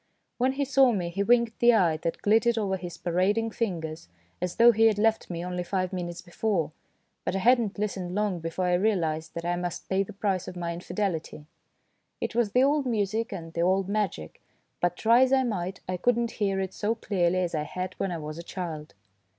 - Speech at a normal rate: No, fast, 220 wpm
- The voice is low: No, high, 190 Hz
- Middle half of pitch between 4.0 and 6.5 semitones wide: Yes, average, 4.3 semitones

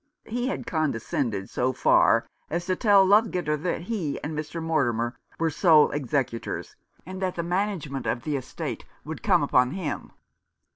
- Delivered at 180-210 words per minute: No, average, 155 wpm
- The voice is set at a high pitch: No, medium, 160 Hz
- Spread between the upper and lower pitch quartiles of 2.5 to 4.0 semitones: No, average, 5.3 semitones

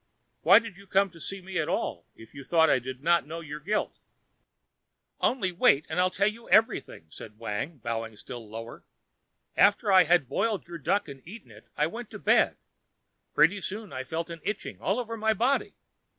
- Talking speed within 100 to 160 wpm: No, average, 200 wpm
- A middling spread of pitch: No, wide, 6.8 semitones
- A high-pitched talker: No, medium, 170 Hz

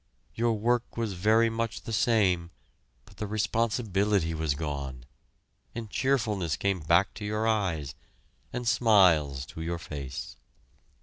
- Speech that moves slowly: Yes, slow, 130 wpm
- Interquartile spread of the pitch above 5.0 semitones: Yes, wide, 5.5 semitones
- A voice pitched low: Yes, low, 100 Hz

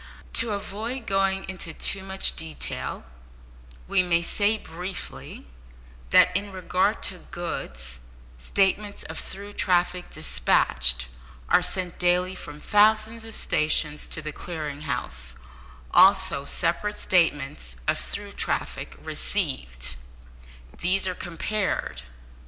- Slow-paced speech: Yes, slow, 110 wpm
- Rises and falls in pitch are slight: No, average, 4.4 semitones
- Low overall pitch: No, medium, 180 Hz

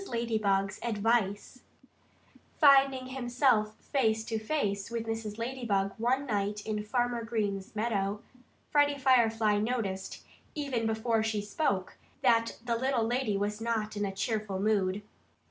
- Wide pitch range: No, average, 2.8 semitones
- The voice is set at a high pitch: Yes, high, 225 Hz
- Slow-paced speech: Yes, slow, 130 wpm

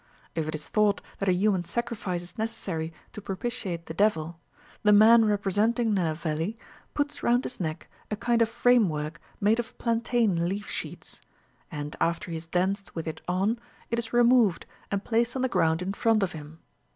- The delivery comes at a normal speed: Yes, average, 180 wpm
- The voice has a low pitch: No, high, 200 Hz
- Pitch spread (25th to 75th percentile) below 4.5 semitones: No, wide, 5.4 semitones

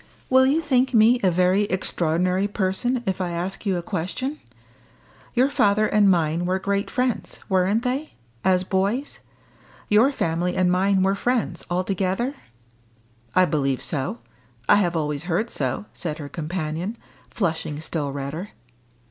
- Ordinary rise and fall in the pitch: Yes, average, 4.1 semitones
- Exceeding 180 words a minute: No, average, 145 wpm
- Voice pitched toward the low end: No, medium, 185 Hz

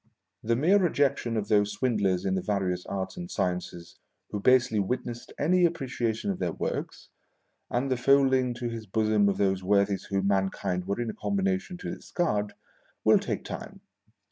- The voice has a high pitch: No, low, 110 Hz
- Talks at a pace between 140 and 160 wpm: No, average, 170 wpm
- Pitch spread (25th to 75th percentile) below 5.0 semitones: No, average, 5.3 semitones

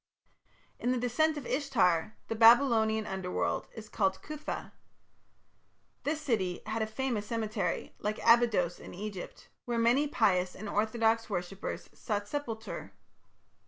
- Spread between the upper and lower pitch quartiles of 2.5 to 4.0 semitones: Yes, average, 3.1 semitones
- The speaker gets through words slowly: Yes, slow, 125 wpm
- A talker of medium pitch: No, high, 220 Hz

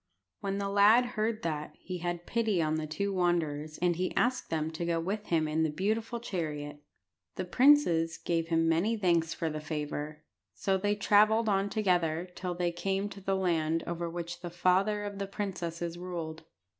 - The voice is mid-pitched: Yes, medium, 175 Hz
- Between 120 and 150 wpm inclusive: No, average, 185 wpm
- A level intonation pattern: No, average, 3.6 semitones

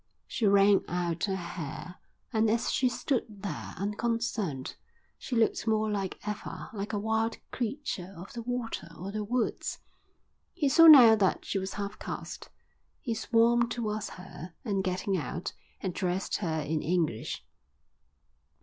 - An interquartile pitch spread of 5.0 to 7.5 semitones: No, average, 3.9 semitones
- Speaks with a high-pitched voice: Yes, high, 205 Hz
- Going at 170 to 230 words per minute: No, average, 145 wpm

